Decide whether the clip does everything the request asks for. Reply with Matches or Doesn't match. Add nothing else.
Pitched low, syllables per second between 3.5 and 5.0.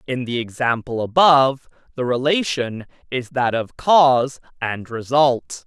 Matches